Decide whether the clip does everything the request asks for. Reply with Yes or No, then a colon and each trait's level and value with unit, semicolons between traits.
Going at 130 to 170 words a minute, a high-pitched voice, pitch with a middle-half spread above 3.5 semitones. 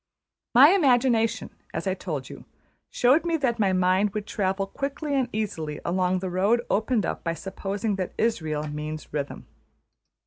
Yes: average, 160 wpm; high, 200 Hz; average, 4.8 semitones